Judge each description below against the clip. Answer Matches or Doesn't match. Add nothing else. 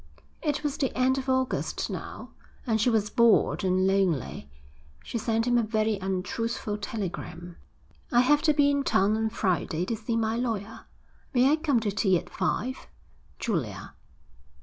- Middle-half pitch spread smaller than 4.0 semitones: Doesn't match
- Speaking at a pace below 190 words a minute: Matches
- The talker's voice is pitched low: Doesn't match